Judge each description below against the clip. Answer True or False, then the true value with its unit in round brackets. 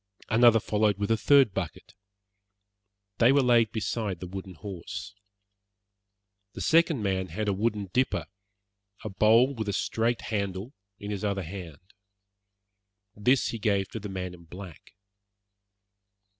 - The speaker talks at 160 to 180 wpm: False (140 wpm)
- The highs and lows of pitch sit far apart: False (3.3 semitones)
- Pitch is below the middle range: True (105 Hz)